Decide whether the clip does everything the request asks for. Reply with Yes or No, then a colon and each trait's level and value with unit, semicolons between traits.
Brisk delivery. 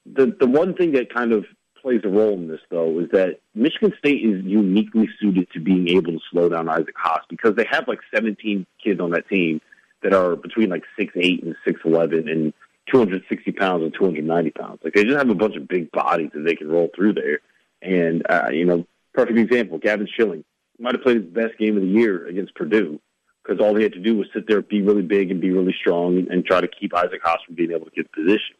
Yes: fast, 250 wpm